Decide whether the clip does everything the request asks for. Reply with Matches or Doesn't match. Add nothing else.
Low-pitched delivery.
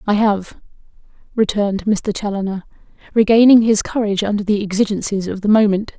Doesn't match